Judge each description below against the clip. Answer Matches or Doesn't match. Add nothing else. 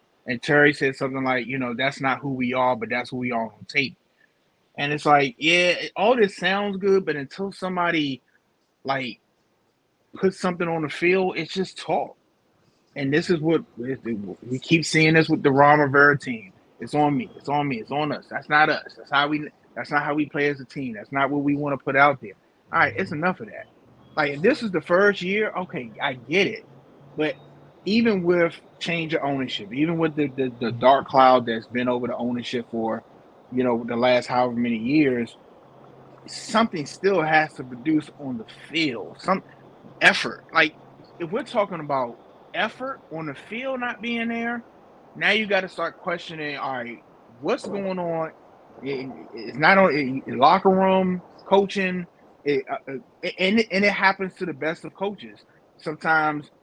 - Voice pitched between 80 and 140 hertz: Doesn't match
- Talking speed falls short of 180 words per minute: Doesn't match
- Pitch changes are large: Matches